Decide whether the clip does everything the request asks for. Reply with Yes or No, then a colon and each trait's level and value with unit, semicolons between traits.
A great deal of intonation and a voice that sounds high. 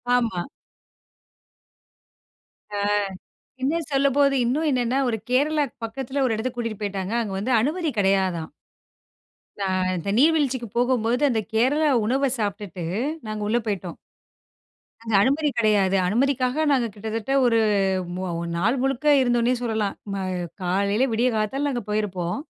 No: average, 4.7 semitones; high, 235 Hz